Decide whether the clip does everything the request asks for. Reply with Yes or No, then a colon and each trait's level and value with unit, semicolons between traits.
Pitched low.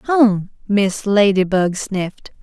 No: high, 200 Hz